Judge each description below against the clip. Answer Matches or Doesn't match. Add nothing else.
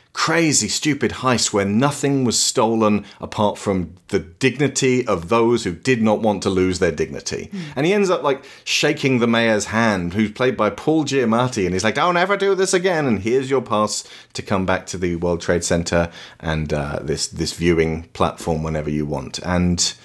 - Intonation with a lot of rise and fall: Matches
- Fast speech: Doesn't match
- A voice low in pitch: Matches